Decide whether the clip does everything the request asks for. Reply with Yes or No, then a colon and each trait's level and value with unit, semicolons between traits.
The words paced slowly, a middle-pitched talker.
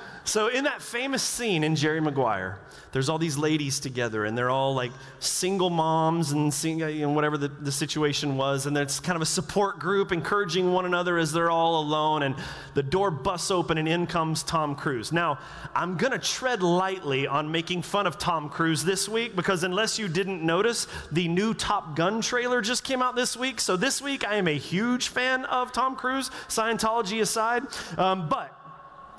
No: average, 195 wpm; medium, 170 Hz